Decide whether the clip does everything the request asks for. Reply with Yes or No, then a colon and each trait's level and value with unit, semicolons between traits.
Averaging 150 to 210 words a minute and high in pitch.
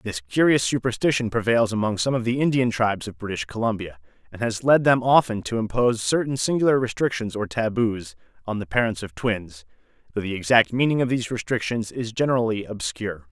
No: average, 180 wpm; low, 115 Hz